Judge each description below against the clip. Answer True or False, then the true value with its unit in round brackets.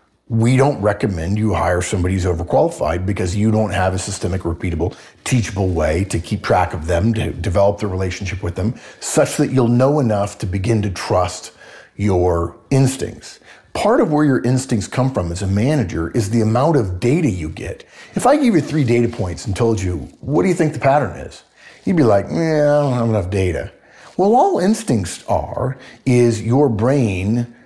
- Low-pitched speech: True (110 Hz)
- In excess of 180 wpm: True (195 wpm)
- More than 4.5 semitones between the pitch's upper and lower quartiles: True (5.2 semitones)